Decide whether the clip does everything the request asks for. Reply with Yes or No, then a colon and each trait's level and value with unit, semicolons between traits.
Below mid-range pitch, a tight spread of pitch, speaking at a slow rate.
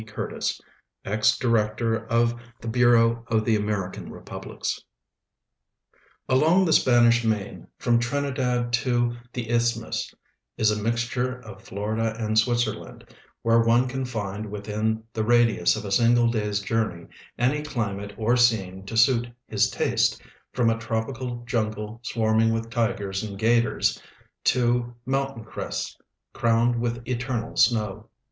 Yes: low, 115 Hz; narrow, 1.9 semitones; slow, 130 wpm